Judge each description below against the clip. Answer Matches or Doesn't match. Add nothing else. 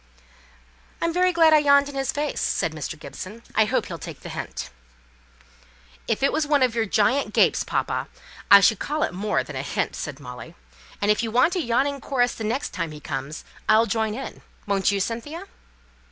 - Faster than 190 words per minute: Matches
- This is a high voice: Matches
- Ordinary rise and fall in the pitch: Doesn't match